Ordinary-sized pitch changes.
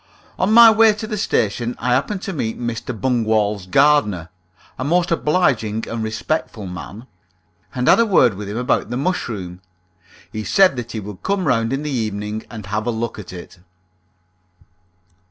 No: wide, 6.0 semitones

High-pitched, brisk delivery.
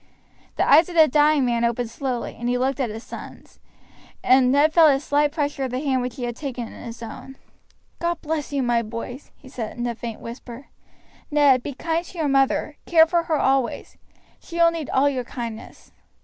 Yes: very high, 270 Hz; fast, 210 wpm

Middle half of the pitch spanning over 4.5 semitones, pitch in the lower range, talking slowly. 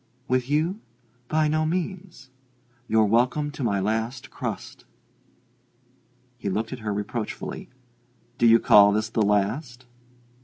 Yes: wide, 5.6 semitones; low, 120 Hz; slow, 125 wpm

